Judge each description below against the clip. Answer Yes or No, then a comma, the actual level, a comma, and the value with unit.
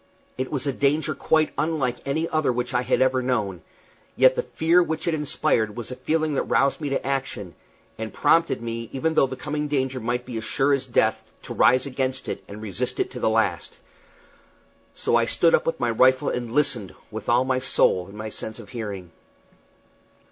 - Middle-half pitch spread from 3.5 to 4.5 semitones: Yes, average, 3.9 semitones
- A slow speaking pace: No, average, 200 wpm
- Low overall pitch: Yes, low, 130 Hz